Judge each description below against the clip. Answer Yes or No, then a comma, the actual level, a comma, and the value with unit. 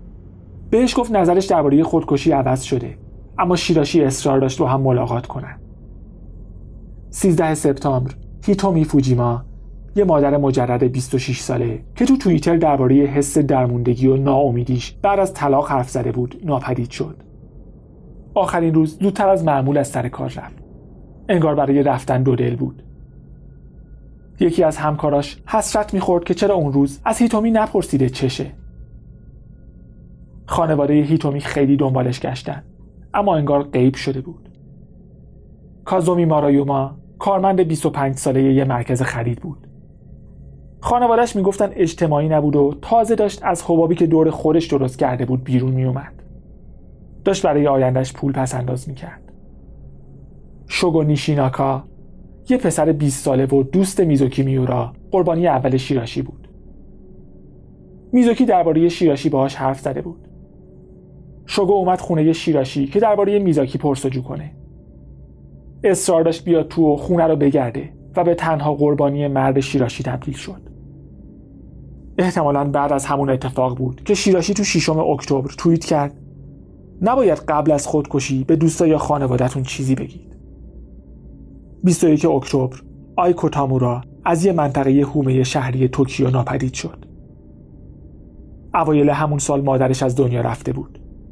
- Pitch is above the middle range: No, medium, 140 Hz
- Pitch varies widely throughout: No, average, 4.3 semitones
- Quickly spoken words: No, average, 130 wpm